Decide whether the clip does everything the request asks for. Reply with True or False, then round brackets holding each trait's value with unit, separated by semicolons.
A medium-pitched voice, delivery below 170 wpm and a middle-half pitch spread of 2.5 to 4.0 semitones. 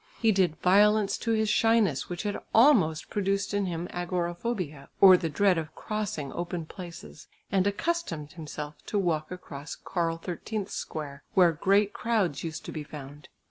False (180 Hz; 160 wpm; 4.4 semitones)